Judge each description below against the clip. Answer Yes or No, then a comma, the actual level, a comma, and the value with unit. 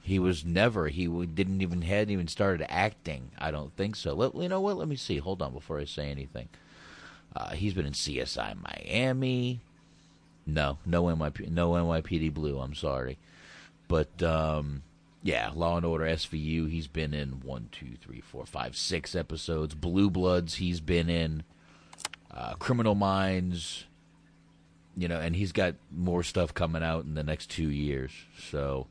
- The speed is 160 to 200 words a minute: Yes, average, 170 wpm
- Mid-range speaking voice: No, very low, 85 Hz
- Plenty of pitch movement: No, average, 3.1 semitones